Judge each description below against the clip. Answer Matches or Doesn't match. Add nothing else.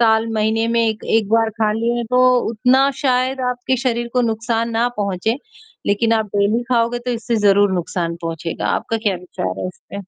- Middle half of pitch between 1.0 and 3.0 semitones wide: Matches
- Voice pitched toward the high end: Matches